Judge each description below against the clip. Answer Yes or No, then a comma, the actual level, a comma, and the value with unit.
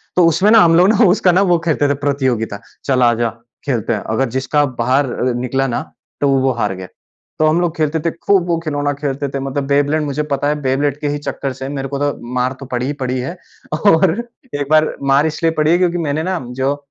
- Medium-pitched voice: Yes, medium, 145 Hz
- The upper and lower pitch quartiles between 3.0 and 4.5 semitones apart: Yes, average, 3.3 semitones